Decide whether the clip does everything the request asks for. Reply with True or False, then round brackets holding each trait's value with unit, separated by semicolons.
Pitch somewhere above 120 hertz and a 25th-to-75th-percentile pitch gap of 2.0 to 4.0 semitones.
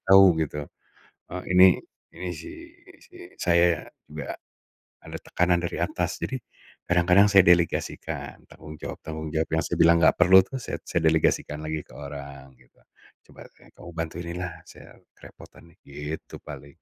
False (85 Hz; 2.6 semitones)